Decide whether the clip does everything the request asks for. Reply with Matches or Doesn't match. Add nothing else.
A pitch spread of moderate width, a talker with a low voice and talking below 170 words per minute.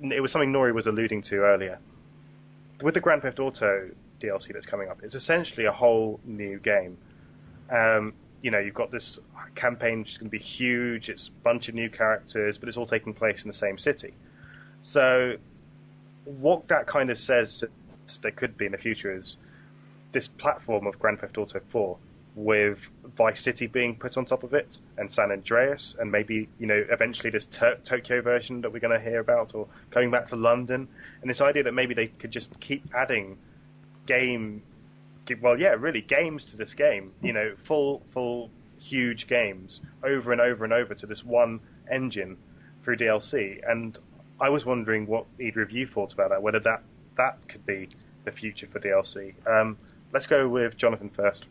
Doesn't match